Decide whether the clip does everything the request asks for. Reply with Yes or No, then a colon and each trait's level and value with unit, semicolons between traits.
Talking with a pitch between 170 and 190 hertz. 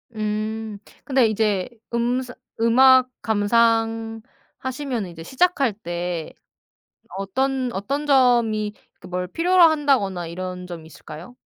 No: high, 225 Hz